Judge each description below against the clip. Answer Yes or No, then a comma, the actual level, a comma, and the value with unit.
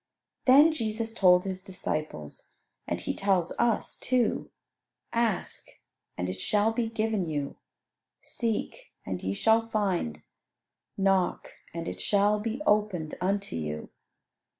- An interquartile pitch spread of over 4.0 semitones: Yes, average, 5.1 semitones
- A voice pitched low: No, high, 200 Hz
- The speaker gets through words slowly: Yes, slow, 125 wpm